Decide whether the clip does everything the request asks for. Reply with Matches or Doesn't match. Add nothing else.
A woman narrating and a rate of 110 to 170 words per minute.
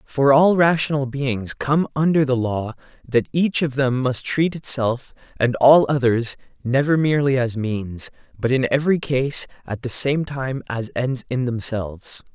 Doesn't match